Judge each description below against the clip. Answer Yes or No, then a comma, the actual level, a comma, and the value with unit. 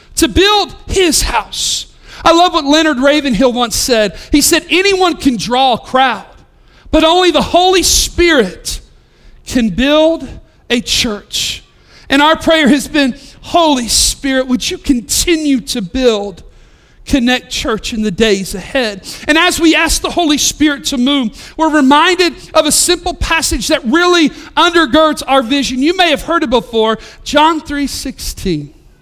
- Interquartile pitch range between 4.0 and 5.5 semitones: Yes, average, 4.5 semitones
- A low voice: No, very high, 290 Hz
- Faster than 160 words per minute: No, average, 155 wpm